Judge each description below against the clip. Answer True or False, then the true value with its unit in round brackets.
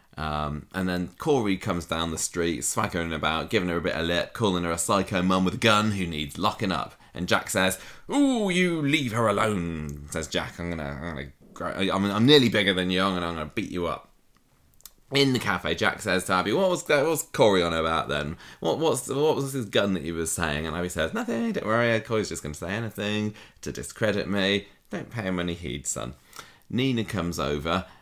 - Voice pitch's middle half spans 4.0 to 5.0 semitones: True (4.7 semitones)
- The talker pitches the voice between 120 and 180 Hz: False (95 Hz)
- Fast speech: True (220 wpm)